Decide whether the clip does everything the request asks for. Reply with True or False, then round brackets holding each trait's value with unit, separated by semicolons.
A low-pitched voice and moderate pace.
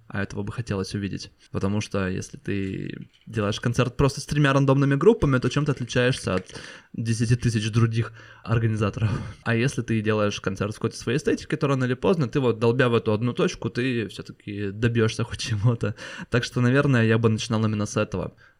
False (115 Hz; 190 wpm)